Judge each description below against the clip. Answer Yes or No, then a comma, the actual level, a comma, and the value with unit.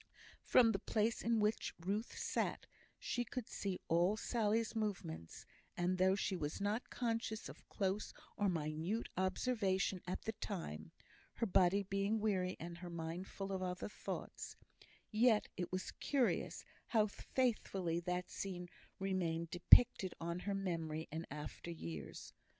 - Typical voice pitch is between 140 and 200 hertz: Yes, high, 190 Hz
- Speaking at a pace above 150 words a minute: No, average, 145 wpm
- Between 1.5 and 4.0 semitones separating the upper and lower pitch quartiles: Yes, average, 3.7 semitones